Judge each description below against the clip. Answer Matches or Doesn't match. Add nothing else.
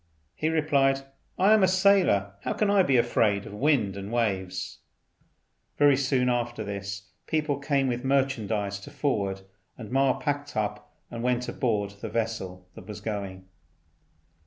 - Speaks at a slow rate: Doesn't match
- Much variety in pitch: Matches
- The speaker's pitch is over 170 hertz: Doesn't match